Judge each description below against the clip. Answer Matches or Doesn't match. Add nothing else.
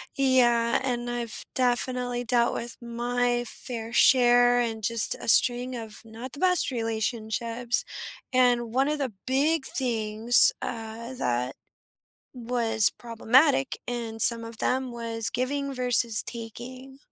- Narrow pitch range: Matches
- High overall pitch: Matches